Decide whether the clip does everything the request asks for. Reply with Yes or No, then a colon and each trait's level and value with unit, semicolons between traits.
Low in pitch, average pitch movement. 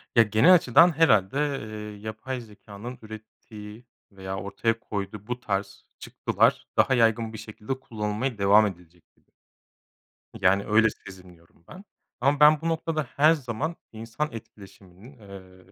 Yes: low, 110 Hz; average, 4.3 semitones